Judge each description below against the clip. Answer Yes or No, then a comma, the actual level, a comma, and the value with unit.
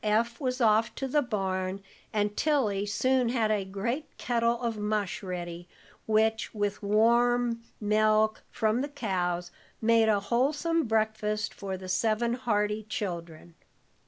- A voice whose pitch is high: Yes, high, 215 Hz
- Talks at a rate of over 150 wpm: No, slow, 135 wpm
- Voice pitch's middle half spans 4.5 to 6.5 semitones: No, average, 2.9 semitones